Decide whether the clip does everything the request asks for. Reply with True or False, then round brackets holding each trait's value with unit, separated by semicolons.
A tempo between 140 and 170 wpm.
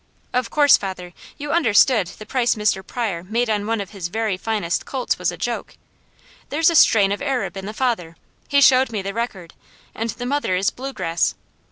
False (195 wpm)